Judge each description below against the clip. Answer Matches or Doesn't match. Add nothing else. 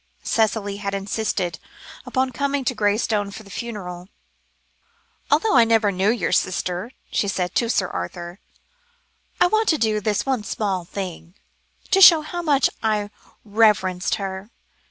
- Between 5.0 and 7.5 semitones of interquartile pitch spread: Doesn't match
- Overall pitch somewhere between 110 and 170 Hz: Doesn't match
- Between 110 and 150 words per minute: Matches